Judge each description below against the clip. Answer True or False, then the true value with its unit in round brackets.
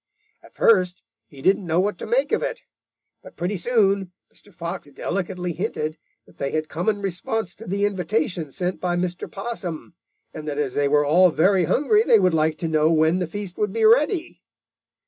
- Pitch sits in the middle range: True (180 Hz)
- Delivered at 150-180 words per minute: False (195 wpm)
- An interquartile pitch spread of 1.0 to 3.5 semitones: False (4.3 semitones)